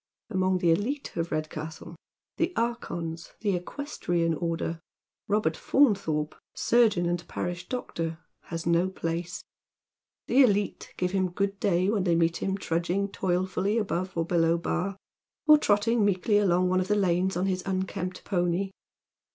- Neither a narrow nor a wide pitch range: Yes, average, 3.0 semitones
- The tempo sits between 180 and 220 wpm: No, average, 160 wpm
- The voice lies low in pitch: No, medium, 185 Hz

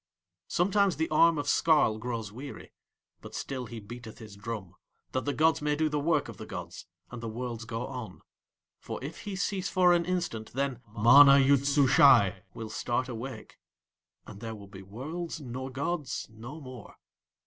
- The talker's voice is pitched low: Yes, low, 130 Hz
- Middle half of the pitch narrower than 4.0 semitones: No, average, 5.2 semitones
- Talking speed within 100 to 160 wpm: No, average, 175 wpm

